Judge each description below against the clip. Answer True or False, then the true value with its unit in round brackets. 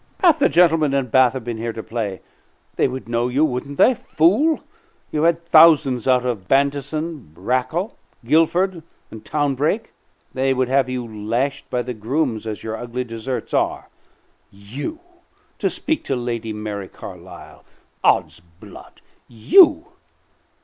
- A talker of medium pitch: False (130 Hz)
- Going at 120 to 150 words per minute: True (145 wpm)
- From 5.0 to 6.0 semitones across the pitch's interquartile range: True (5.3 semitones)